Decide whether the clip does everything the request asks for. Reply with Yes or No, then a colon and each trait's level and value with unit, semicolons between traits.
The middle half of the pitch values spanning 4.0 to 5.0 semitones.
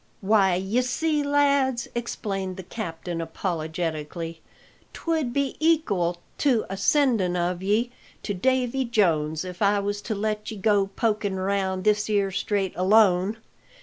Yes: average, 4.5 semitones